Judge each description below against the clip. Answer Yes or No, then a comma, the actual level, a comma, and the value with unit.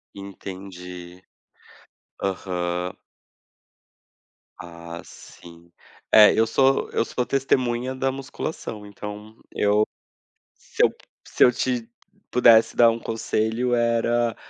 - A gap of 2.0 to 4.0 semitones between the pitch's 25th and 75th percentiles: No, average, 4.6 semitones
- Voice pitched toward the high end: No, low, 110 Hz